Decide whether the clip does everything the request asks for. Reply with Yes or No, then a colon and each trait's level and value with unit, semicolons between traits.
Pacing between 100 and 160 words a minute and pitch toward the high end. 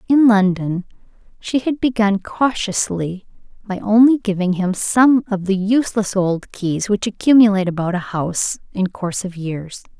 Yes: average, 150 wpm; high, 200 Hz